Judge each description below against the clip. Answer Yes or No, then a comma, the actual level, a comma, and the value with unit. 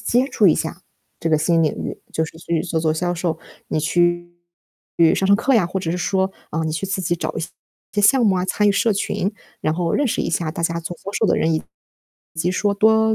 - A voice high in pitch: No, medium, 175 Hz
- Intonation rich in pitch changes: No, average, 3.6 semitones